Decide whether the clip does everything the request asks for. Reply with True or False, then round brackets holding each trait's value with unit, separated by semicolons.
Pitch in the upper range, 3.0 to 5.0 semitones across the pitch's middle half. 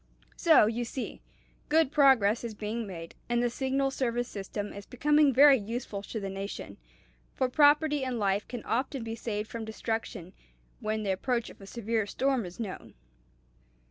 True (230 Hz; 4.2 semitones)